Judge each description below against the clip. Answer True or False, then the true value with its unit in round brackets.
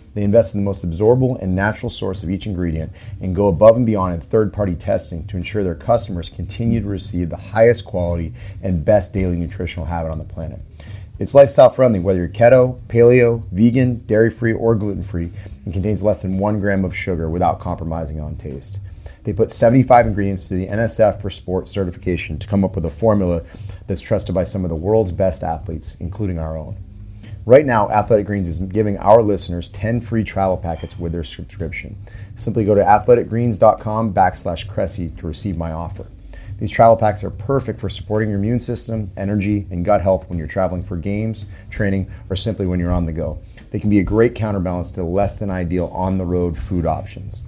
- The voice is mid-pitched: False (100 Hz)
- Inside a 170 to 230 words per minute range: True (200 wpm)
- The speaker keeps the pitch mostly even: False (3.3 semitones)